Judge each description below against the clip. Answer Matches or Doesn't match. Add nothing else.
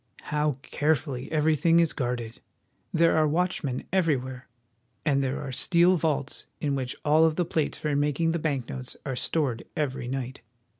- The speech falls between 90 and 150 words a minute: Doesn't match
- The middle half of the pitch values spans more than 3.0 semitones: Matches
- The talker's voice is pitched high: Doesn't match